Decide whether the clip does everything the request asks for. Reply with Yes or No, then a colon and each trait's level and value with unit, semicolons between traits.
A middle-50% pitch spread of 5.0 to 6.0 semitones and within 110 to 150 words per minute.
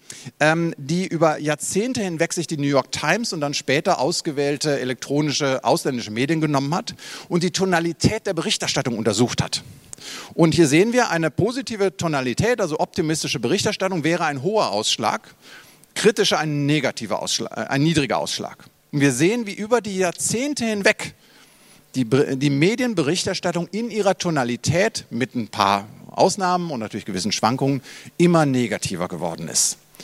Yes: average, 5.3 semitones; average, 140 wpm